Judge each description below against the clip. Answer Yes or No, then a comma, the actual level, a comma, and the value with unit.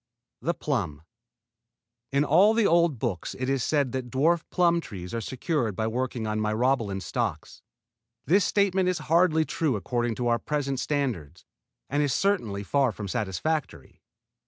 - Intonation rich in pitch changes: Yes, wide, 6.4 semitones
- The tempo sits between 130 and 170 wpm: Yes, average, 155 wpm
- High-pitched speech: No, low, 130 Hz